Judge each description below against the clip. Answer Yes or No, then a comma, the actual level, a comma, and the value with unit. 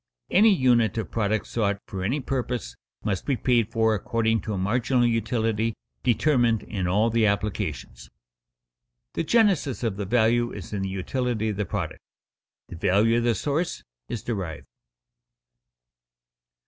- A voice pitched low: Yes, low, 115 Hz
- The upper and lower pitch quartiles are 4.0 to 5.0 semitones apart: No, average, 3.1 semitones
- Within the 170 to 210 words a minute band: No, average, 150 wpm